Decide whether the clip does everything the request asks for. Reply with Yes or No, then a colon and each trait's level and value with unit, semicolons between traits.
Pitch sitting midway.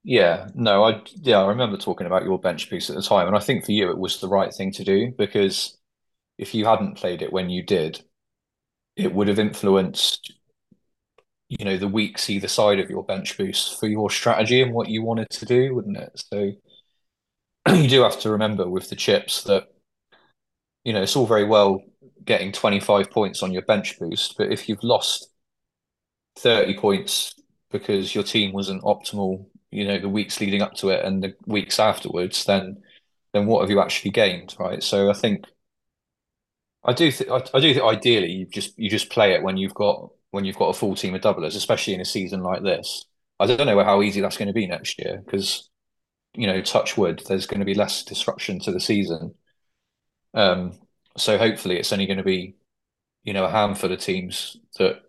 No: low, 100 Hz